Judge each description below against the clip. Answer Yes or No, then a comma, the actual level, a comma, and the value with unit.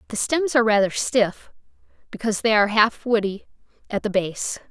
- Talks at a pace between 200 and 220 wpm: No, average, 165 wpm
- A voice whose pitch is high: Yes, high, 220 Hz